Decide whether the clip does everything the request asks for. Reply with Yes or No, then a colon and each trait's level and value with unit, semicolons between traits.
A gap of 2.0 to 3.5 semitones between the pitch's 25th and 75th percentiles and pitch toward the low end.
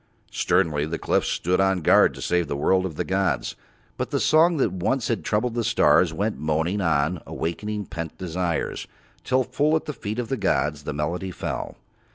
No: average, 5.1 semitones; very low, 90 Hz